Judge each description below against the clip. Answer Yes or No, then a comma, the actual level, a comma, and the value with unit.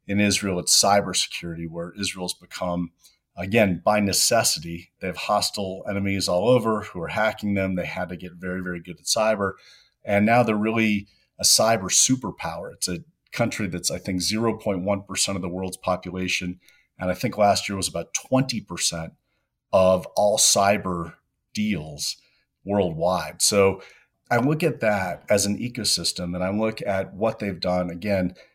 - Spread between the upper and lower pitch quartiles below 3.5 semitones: Yes, average, 2.7 semitones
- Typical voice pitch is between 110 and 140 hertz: No, very low, 95 Hz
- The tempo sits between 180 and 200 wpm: No, average, 160 wpm